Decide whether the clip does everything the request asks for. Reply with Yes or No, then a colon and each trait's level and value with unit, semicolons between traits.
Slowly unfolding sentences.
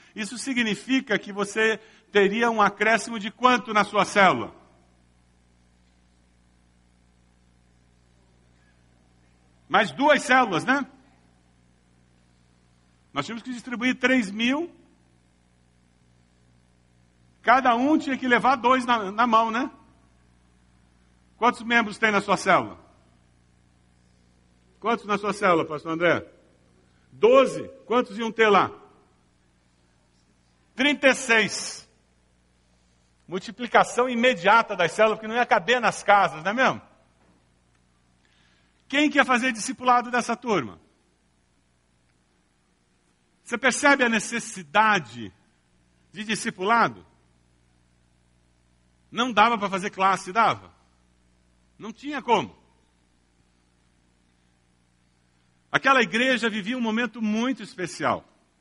Yes: slow, 95 wpm